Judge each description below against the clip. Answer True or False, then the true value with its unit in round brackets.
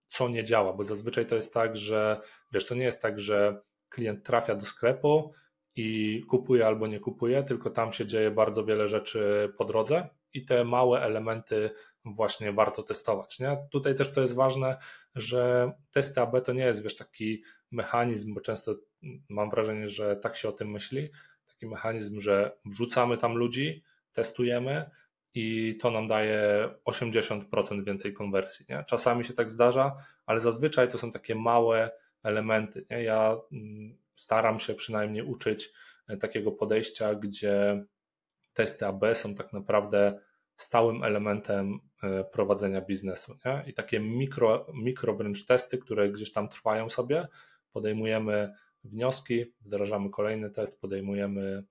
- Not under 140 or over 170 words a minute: True (145 wpm)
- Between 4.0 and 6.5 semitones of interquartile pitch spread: False (2.9 semitones)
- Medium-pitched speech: False (110 Hz)